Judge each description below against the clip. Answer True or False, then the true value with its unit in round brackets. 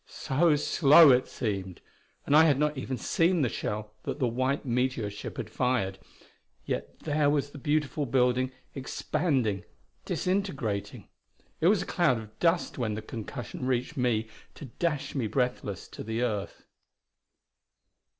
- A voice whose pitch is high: False (130 Hz)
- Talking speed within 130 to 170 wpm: True (150 wpm)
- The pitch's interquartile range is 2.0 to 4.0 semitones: False (4.9 semitones)